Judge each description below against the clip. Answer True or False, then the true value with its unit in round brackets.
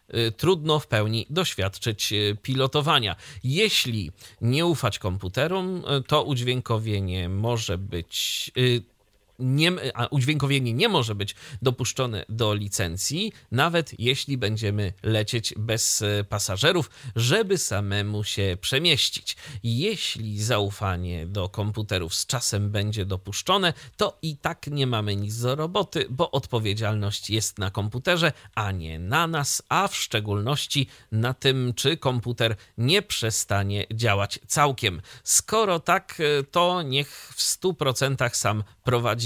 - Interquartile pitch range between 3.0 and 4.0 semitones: False (5.3 semitones)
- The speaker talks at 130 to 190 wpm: False (120 wpm)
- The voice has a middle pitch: False (120 Hz)